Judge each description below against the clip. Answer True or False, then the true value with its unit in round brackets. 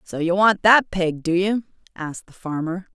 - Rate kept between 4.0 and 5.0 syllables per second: True (4.9 syllables/s)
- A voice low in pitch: False (185 Hz)